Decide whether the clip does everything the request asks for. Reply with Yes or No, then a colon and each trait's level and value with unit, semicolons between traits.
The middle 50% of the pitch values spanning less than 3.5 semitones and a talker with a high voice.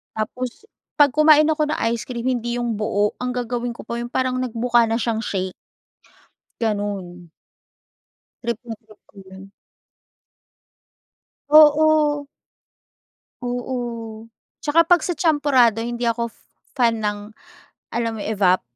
Yes: average, 2.9 semitones; high, 235 Hz